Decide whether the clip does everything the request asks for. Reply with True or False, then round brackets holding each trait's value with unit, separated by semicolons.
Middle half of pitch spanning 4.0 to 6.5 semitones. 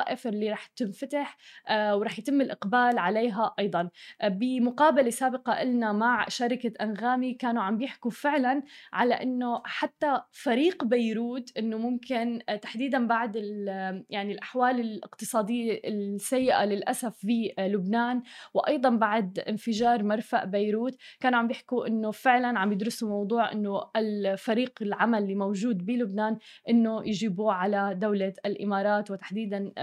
False (2.9 semitones)